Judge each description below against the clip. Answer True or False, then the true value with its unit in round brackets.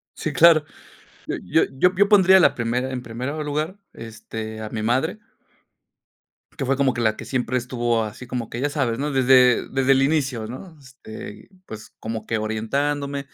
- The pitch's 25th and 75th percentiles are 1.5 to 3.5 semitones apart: False (3.9 semitones)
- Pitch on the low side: True (130 Hz)